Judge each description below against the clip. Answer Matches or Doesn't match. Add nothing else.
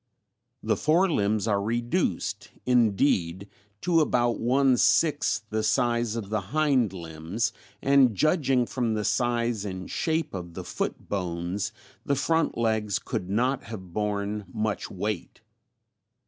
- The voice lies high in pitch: Doesn't match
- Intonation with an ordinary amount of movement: Matches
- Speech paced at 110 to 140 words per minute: Matches